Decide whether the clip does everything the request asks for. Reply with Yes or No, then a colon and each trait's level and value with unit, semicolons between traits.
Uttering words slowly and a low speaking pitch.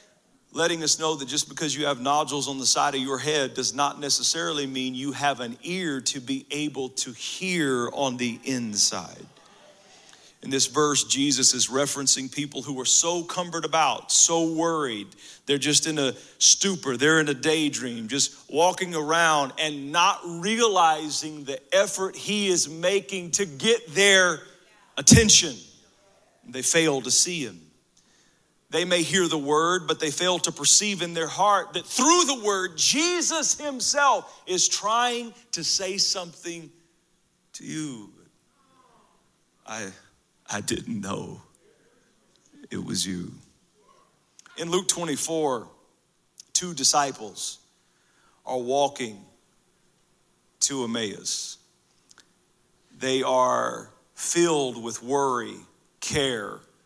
No: slow, 130 wpm; medium, 155 Hz